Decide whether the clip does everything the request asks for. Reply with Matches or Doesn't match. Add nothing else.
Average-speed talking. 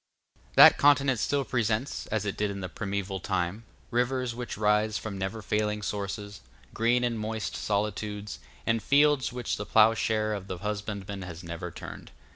Matches